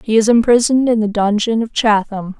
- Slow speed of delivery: No, average, 200 wpm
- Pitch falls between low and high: No, high, 220 Hz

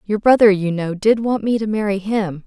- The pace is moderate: No, fast, 245 wpm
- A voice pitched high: Yes, high, 205 Hz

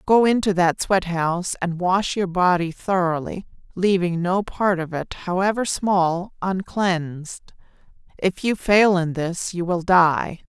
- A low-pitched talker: No, medium, 180 Hz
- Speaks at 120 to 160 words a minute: Yes, average, 150 wpm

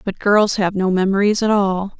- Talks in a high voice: Yes, high, 200 Hz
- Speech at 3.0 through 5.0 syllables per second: Yes, 4.9 syllables/s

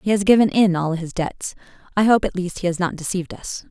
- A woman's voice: Yes, female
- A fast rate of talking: Yes, fast, 260 wpm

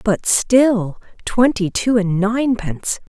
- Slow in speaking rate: Yes, slow, 95 wpm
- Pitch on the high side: Yes, high, 215 Hz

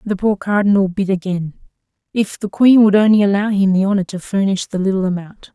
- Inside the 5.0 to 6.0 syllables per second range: Yes, 5.8 syllables/s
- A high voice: Yes, high, 195 Hz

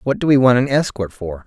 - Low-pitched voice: Yes, low, 120 Hz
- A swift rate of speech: Yes, fast, 285 wpm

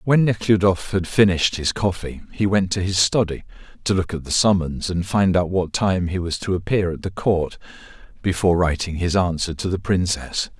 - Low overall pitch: Yes, very low, 90 Hz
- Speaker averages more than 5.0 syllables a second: Yes, 5.2 syllables/s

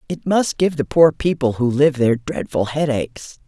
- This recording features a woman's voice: Yes, female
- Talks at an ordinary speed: Yes, average, 190 wpm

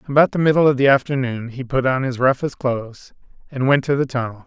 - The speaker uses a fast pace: Yes, fast, 230 wpm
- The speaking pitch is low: Yes, low, 130 Hz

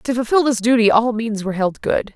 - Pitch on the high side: Yes, high, 230 Hz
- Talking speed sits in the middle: No, fast, 250 wpm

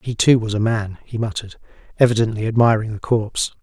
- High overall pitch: No, low, 110 Hz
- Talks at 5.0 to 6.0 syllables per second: No, 6.3 syllables/s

